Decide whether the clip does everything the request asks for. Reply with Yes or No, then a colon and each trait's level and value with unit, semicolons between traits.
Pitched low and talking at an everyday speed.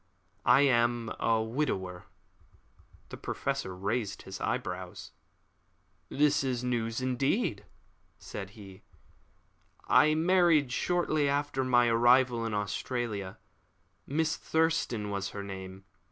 No: low, 120 Hz; slow, 105 wpm